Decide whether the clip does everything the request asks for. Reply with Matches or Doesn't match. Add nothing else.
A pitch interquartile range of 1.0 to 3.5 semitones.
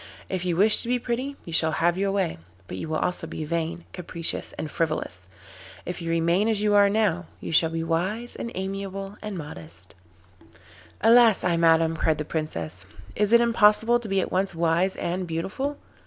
Doesn't match